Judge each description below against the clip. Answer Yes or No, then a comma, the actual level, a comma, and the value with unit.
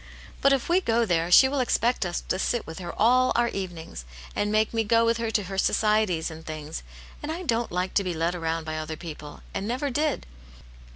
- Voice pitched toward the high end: Yes, high, 205 Hz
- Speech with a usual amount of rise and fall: No, wide, 6.1 semitones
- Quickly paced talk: Yes, fast, 225 wpm